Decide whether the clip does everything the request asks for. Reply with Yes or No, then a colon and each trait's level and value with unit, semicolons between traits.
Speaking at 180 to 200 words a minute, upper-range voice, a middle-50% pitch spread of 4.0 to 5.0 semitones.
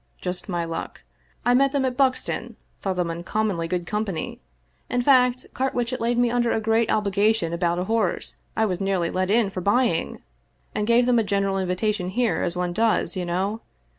Yes: average, 195 wpm; high, 205 Hz; average, 4.7 semitones